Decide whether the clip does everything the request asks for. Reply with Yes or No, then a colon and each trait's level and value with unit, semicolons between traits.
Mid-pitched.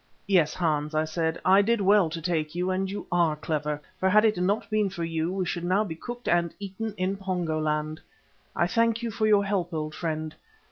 Yes: medium, 180 Hz